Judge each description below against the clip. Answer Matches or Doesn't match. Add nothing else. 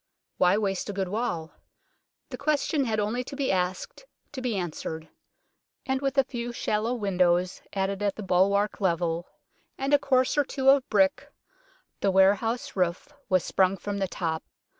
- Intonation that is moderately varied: Doesn't match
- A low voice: Doesn't match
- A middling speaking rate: Matches